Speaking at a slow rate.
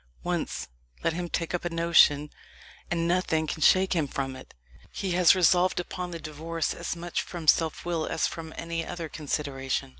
No: average, 180 wpm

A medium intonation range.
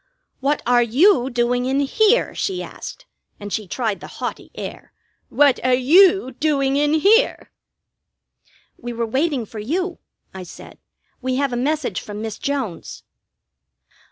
Yes: average, 4.3 semitones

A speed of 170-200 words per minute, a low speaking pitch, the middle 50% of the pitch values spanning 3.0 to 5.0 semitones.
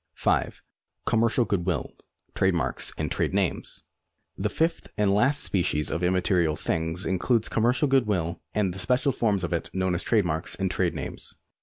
Yes: average, 180 wpm; very low, 95 Hz; average, 4.3 semitones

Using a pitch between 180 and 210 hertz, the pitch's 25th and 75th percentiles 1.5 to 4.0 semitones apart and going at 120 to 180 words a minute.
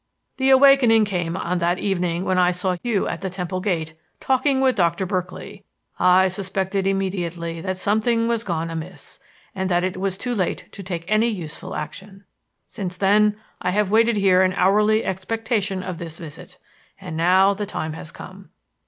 Yes: high, 190 Hz; average, 2.8 semitones; average, 175 wpm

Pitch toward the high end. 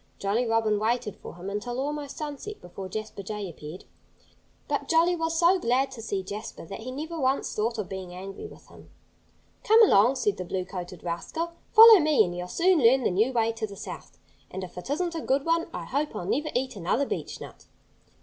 Yes: high, 230 Hz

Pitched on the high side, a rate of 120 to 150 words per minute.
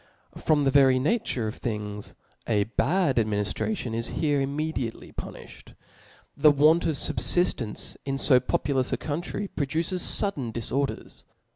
No: low, 135 Hz; slow, 135 wpm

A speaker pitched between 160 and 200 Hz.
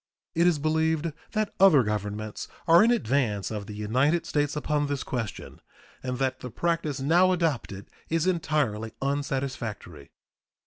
No: medium, 140 Hz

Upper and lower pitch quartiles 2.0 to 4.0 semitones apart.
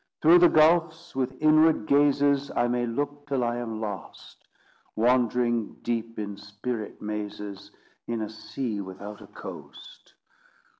No: average, 5.1 semitones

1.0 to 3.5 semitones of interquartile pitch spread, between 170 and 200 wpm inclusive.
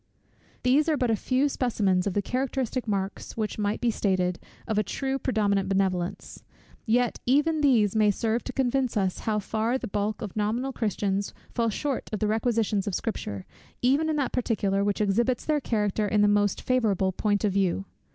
No: average, 3.9 semitones; average, 185 wpm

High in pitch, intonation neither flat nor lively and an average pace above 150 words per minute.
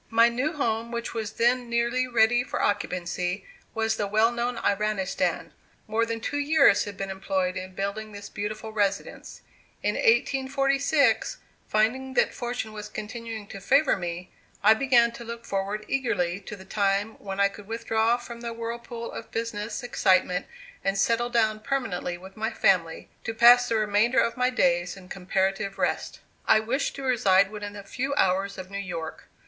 Yes: high, 220 Hz; average, 3.3 semitones; average, 170 wpm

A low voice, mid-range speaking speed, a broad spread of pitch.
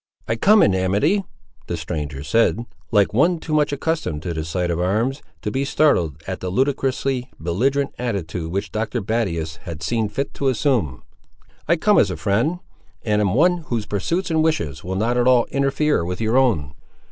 Yes: low, 110 Hz; average, 185 wpm; wide, 7.5 semitones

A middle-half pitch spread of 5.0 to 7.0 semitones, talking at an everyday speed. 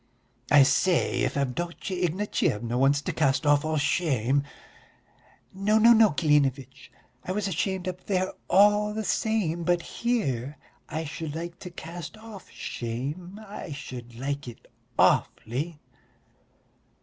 No: average, 5.3 semitones; slow, 130 wpm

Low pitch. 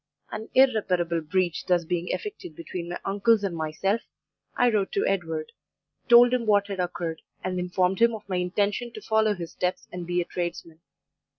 No: medium, 185 Hz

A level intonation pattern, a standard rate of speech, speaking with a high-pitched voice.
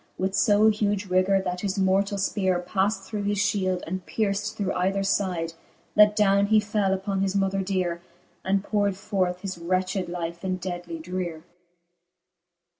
Yes: narrow, 1.8 semitones; average, 160 wpm; high, 195 Hz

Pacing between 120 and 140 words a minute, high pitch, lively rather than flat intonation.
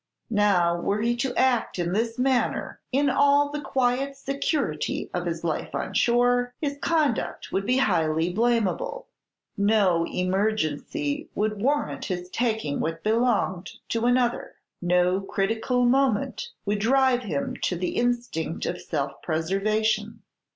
Yes: slow, 135 wpm; high, 220 Hz; wide, 5.7 semitones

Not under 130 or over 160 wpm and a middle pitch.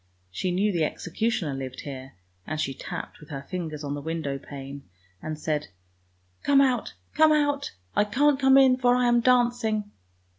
No: average, 185 wpm; medium, 175 Hz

